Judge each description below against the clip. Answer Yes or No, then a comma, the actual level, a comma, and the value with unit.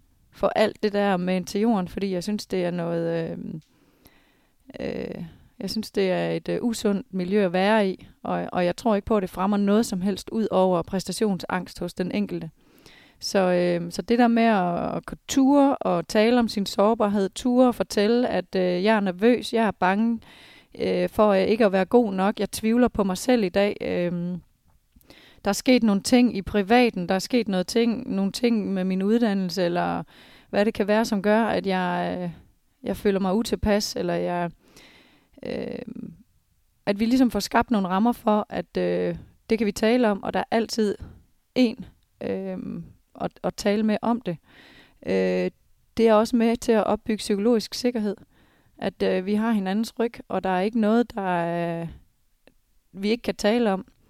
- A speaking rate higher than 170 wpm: Yes, average, 195 wpm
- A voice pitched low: No, high, 205 Hz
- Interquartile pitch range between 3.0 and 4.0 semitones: Yes, average, 3.6 semitones